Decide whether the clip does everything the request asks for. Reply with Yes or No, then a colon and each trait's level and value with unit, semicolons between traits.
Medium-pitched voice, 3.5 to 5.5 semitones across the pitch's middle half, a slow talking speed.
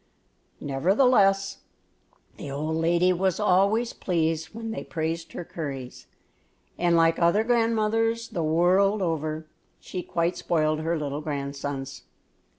Yes: medium, 170 Hz; average, 4.1 semitones; slow, 120 wpm